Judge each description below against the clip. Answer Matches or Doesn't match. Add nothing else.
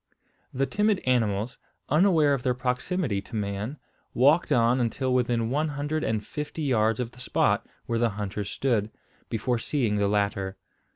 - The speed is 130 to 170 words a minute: Matches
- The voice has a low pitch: Matches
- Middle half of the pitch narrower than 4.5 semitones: Doesn't match